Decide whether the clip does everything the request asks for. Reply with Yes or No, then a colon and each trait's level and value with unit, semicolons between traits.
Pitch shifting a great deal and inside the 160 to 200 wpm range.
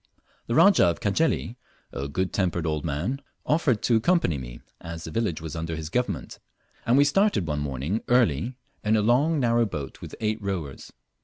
Yes: wide, 7.5 semitones; average, 180 wpm